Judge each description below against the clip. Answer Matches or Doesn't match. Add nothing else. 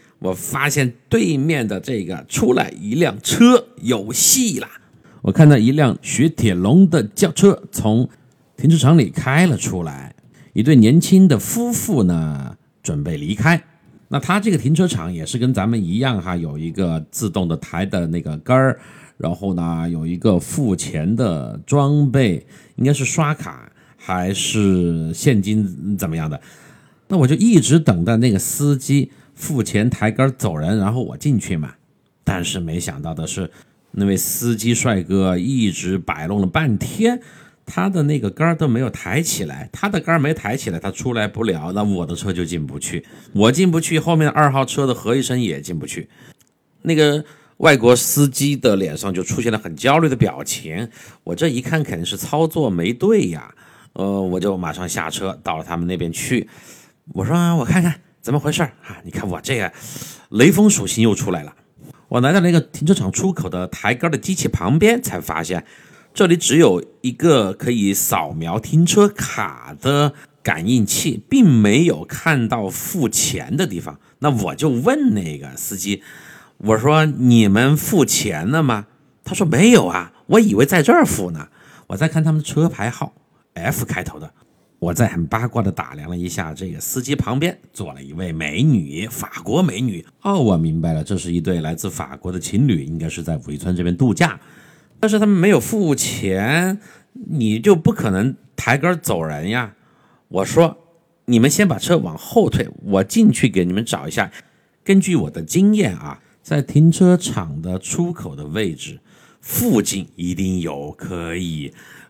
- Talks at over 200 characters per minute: Matches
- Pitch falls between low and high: Doesn't match